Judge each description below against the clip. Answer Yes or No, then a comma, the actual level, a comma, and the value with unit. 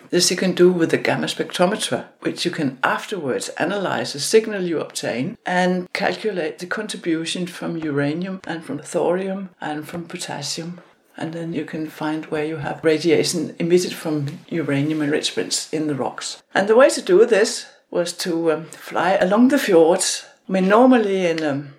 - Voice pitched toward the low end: No, medium, 170 Hz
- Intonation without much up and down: No, average, 3.4 semitones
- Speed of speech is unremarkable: Yes, average, 175 wpm